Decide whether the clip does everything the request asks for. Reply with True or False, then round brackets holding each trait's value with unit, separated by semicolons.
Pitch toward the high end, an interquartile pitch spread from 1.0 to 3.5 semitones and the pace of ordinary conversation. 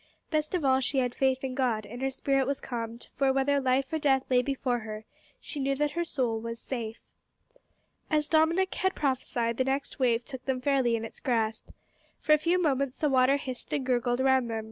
False (265 Hz; 2.5 semitones; 210 wpm)